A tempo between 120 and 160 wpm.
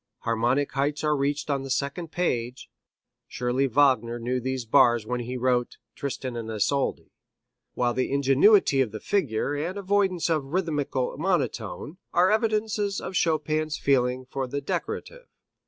Yes: average, 150 wpm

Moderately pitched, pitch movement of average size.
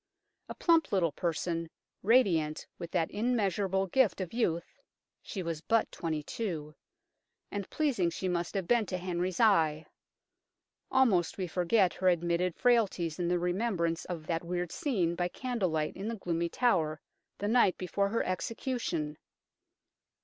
Yes: medium, 180 Hz; average, 4.2 semitones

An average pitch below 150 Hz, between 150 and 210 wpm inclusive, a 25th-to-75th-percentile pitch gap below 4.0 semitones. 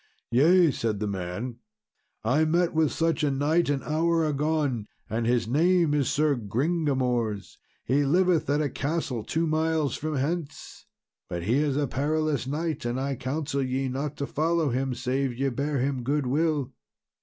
Yes: medium, 140 Hz; average, 165 wpm; average, 3.6 semitones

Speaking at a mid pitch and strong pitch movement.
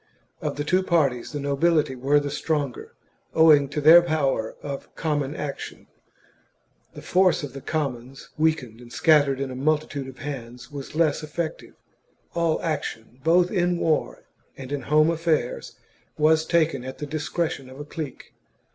No: medium, 145 Hz; average, 2.8 semitones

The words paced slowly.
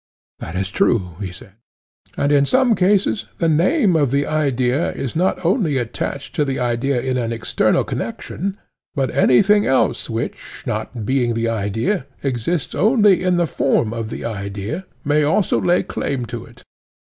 No: average, 165 wpm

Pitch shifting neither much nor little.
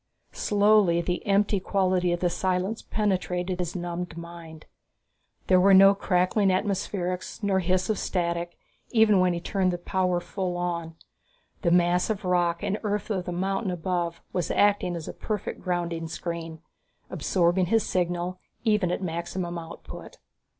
No: narrow, 2.1 semitones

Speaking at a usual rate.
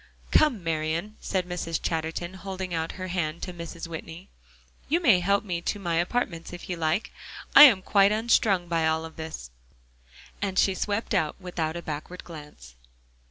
Yes: average, 165 wpm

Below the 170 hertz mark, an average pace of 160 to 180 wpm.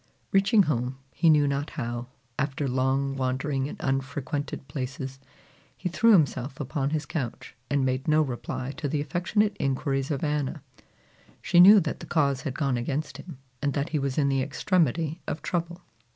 Yes: medium, 140 Hz; average, 170 wpm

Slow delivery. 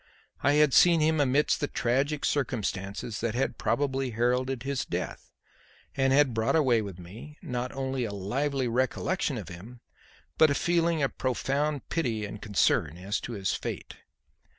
No: average, 160 wpm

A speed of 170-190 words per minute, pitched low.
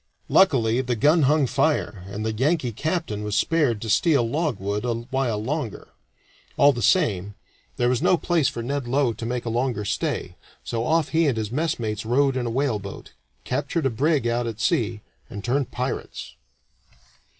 Yes: average, 175 wpm; low, 125 Hz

